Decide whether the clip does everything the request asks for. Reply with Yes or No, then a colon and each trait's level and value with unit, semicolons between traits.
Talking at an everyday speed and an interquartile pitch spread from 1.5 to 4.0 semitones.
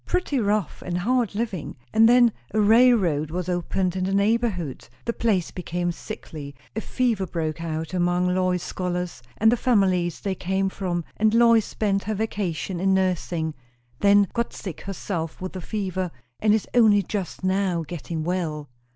Yes: average, 165 wpm; average, 3.5 semitones